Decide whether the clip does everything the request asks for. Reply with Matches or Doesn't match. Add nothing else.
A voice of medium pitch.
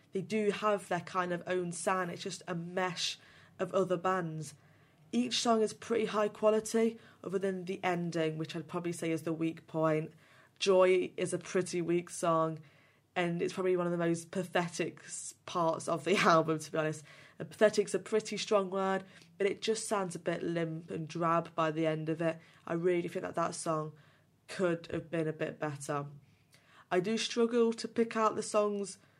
Matches